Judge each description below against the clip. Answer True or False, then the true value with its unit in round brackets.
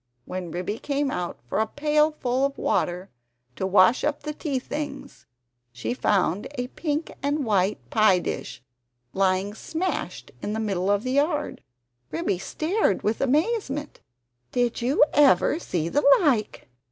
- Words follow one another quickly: False (145 wpm)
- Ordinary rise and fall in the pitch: False (7.4 semitones)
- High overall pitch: True (245 Hz)